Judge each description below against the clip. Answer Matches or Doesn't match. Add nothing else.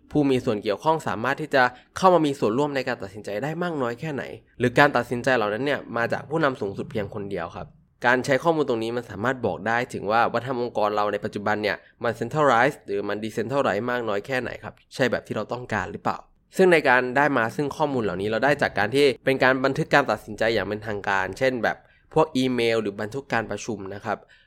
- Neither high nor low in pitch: Doesn't match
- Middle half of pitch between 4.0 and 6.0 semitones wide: Matches